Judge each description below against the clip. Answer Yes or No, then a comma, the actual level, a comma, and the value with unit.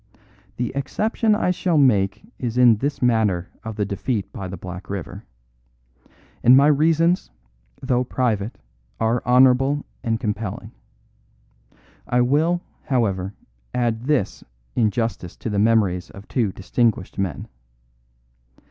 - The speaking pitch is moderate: No, low, 115 Hz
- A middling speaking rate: No, slow, 125 wpm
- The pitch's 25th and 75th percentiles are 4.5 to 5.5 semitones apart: Yes, average, 4.8 semitones